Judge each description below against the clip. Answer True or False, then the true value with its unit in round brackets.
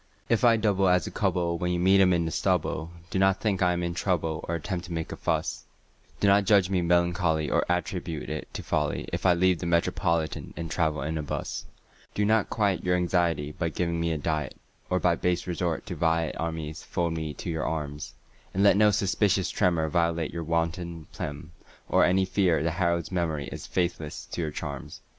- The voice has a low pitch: True (85 Hz)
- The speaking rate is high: True (215 wpm)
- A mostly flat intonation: True (2.2 semitones)